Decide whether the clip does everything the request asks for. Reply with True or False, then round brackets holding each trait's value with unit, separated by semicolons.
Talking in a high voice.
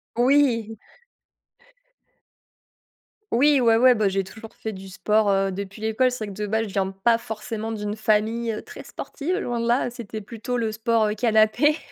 True (220 Hz)